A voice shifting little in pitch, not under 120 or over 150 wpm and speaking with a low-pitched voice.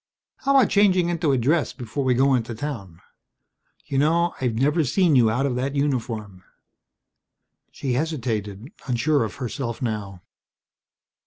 No: average, 4.8 semitones; average, 145 wpm; low, 130 Hz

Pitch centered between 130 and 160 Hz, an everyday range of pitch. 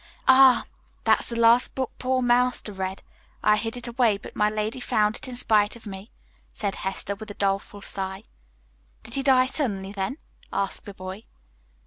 No: high, 215 Hz; average, 3.8 semitones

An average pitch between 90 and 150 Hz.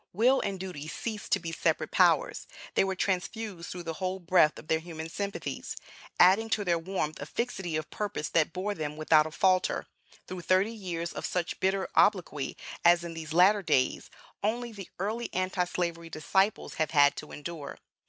No: medium, 180 Hz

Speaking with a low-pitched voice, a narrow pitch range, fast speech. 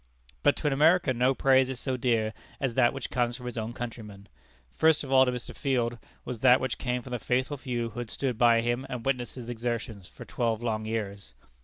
Yes: low, 120 Hz; narrow, 2.3 semitones; fast, 225 wpm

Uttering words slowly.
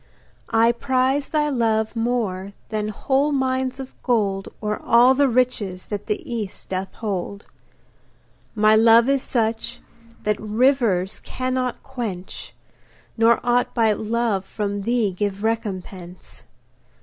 Yes: slow, 125 wpm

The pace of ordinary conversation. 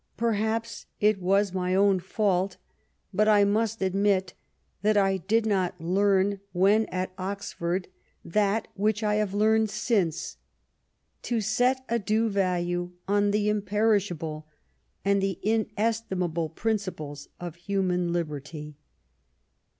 No: slow, 120 wpm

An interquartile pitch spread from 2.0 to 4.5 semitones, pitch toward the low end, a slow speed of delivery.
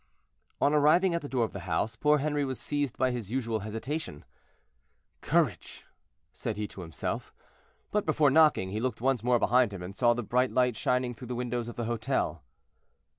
No: average, 4.2 semitones; low, 125 Hz; average, 190 wpm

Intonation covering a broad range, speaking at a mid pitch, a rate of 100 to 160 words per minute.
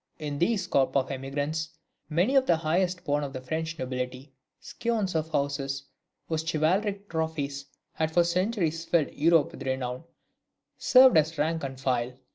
No: average, 3.7 semitones; medium, 155 Hz; average, 155 wpm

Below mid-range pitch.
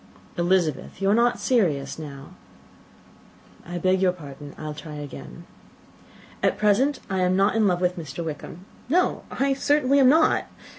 No: medium, 185 Hz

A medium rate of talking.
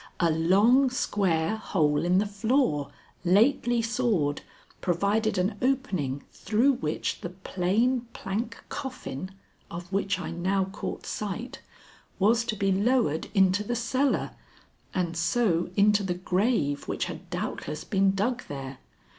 No: slow, 130 wpm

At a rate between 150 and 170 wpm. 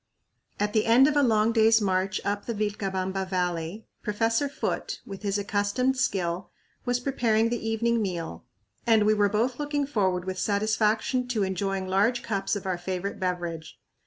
Yes: average, 165 wpm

